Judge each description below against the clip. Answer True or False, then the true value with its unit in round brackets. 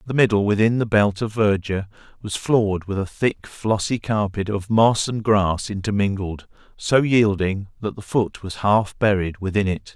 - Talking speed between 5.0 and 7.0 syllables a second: False (4.7 syllables/s)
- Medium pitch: False (105 Hz)